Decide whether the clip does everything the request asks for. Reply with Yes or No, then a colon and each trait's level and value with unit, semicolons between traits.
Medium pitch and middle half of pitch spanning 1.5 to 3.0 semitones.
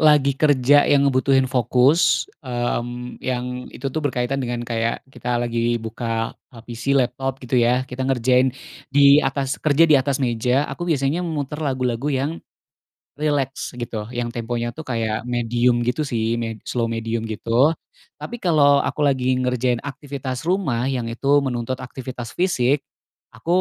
No: low, 125 Hz; narrow, 2.6 semitones